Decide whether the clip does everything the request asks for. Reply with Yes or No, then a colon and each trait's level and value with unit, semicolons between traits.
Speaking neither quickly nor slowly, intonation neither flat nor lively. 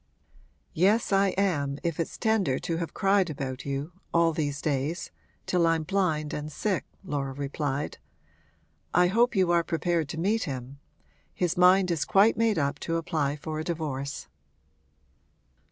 Yes: average, 155 wpm; average, 4.2 semitones